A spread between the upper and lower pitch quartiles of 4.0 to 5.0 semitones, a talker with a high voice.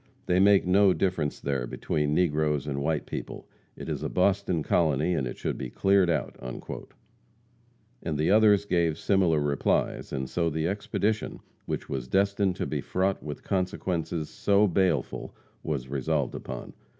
No: average, 4.6 semitones; very low, 85 Hz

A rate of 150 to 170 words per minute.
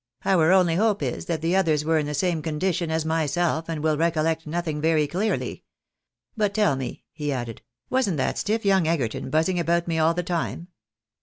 No: fast, 205 wpm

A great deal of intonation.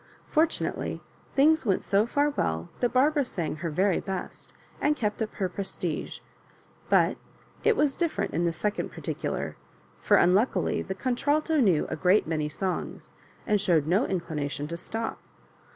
Yes: wide, 8.0 semitones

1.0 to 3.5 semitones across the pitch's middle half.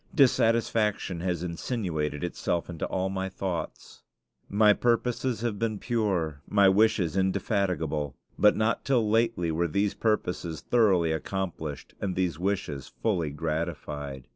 No: average, 4.7 semitones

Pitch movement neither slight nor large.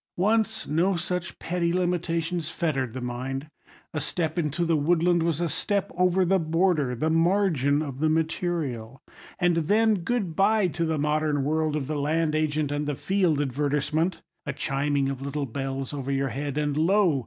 Yes: average, 3.5 semitones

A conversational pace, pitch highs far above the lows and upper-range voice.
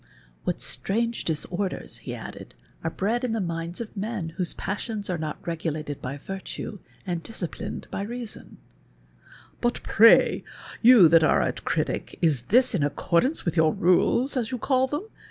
Yes: average, 170 wpm; wide, 6.0 semitones; high, 195 Hz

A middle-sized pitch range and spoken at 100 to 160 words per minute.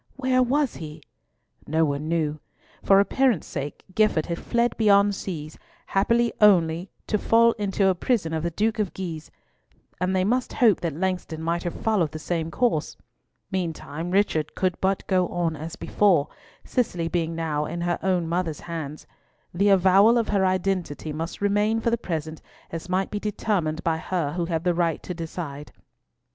No: average, 4.0 semitones; average, 175 wpm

